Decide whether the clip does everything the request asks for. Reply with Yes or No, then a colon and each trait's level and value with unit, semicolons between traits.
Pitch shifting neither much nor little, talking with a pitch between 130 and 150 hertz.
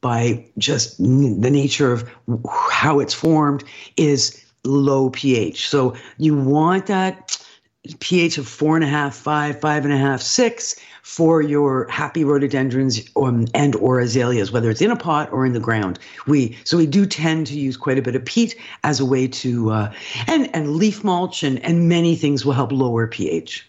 Yes: average, 3.8 semitones; medium, 140 Hz